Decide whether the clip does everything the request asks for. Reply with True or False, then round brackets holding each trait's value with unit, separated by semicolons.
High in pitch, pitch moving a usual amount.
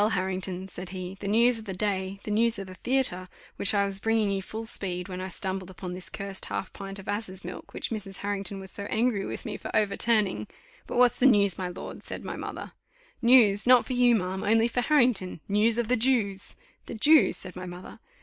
True (200 Hz; 3.2 semitones)